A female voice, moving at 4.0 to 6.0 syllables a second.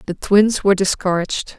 Yes: female; 5.6 syllables/s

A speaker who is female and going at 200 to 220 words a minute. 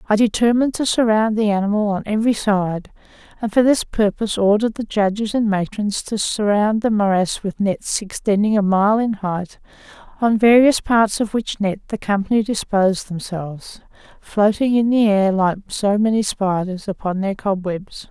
No: female; average, 165 wpm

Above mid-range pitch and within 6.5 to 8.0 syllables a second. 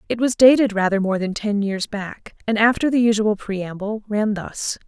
No: high, 210 Hz; 4.7 syllables/s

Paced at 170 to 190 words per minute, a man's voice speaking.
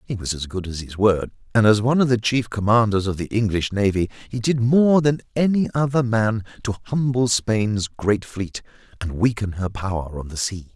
No: fast, 205 wpm; male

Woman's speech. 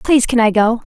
Yes: female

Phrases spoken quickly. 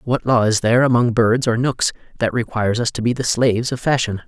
Yes: fast, 240 wpm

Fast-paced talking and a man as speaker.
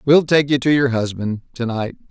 No: average, 170 wpm; male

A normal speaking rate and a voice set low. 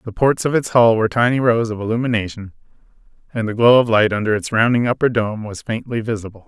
No: fast, 215 wpm; low, 115 Hz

